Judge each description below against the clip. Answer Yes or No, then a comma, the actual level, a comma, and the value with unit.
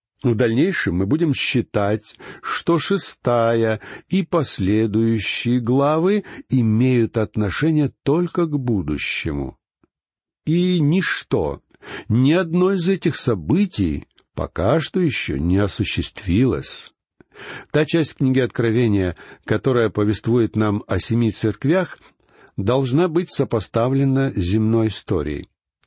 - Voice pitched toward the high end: No, low, 120 Hz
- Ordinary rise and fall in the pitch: No, wide, 6.7 semitones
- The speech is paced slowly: Yes, slow, 100 wpm